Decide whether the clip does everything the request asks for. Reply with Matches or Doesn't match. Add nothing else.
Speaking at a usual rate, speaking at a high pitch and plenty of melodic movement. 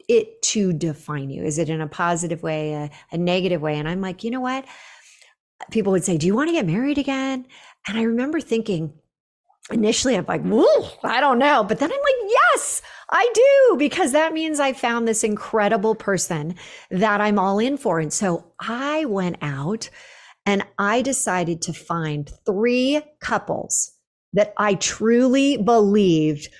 Matches